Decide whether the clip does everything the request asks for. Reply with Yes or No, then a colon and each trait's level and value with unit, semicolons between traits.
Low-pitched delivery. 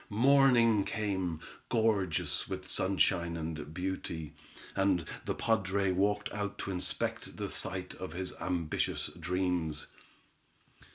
Yes: very low, 95 Hz